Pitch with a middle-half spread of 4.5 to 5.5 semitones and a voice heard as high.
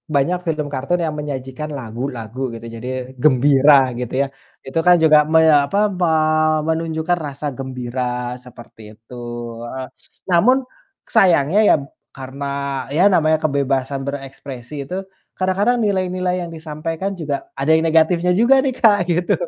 No: average, 5.0 semitones; medium, 150 Hz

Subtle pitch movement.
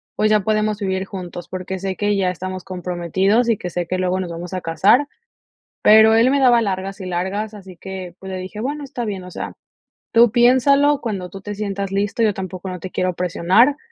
No: average, 3.0 semitones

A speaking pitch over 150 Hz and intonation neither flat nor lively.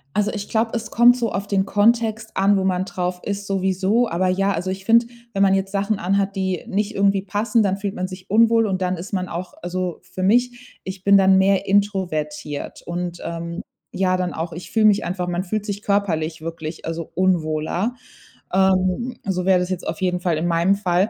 No: high, 190 Hz; narrow, 2.2 semitones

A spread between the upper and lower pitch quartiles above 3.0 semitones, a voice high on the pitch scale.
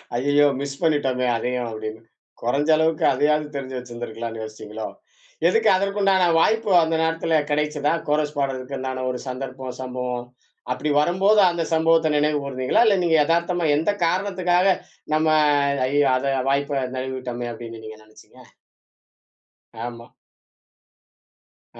No: average, 4.5 semitones; medium, 140 Hz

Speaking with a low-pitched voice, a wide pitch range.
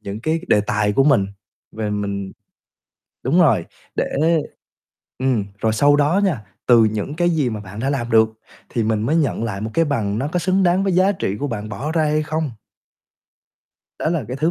Yes: low, 130 Hz; wide, 6.7 semitones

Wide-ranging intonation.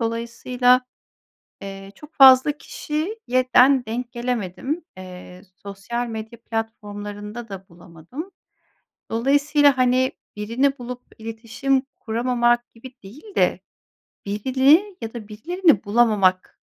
No: average, 4.1 semitones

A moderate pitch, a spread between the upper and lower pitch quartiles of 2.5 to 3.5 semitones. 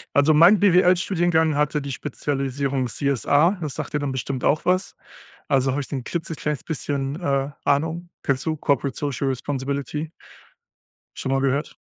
Yes: medium, 145 Hz; average, 2.8 semitones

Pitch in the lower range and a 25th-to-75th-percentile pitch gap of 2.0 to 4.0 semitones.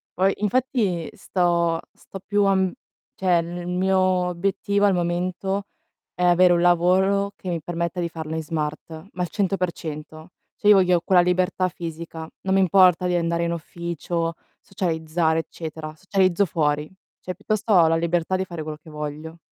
No: medium, 175 Hz; narrow, 2.4 semitones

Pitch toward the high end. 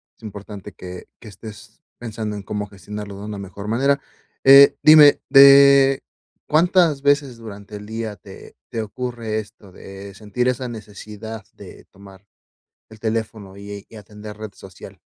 No: low, 110 Hz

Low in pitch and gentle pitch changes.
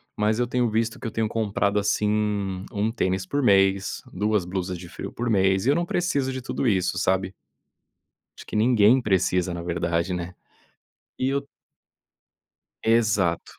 No: low, 105 Hz; average, 3.6 semitones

